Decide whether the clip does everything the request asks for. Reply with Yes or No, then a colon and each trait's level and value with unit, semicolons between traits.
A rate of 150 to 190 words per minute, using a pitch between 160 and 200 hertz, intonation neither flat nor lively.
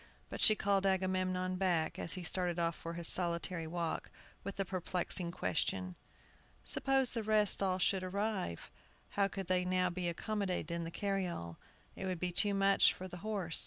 No: average, 175 wpm; medium, 185 Hz; narrow, 2.3 semitones